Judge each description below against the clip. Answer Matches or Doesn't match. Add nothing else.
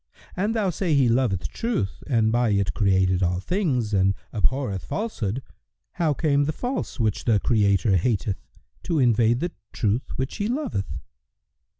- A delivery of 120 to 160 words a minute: Matches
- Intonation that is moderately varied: Doesn't match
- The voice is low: Matches